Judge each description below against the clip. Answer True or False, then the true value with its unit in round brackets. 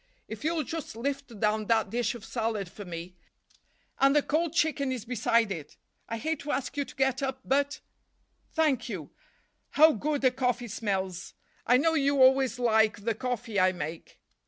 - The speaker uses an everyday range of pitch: True (4.5 semitones)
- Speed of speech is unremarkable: True (170 wpm)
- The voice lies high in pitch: True (245 Hz)